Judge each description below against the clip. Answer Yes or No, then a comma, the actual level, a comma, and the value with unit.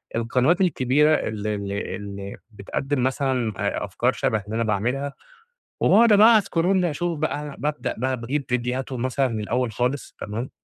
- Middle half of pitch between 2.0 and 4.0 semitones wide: No, average, 4.9 semitones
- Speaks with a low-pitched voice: Yes, low, 130 Hz